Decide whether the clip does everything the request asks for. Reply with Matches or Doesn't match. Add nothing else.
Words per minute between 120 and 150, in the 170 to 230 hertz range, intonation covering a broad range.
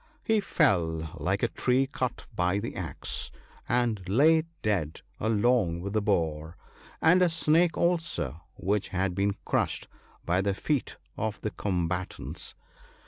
Doesn't match